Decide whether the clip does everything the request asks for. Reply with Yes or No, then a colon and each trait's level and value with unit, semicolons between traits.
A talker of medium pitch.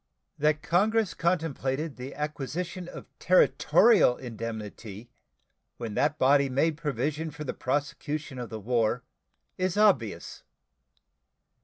Yes: medium, 145 Hz